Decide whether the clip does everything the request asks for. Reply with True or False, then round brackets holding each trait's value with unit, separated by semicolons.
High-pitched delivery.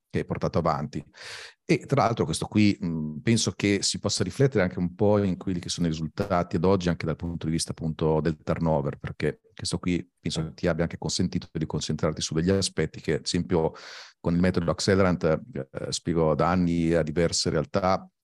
False (85 Hz)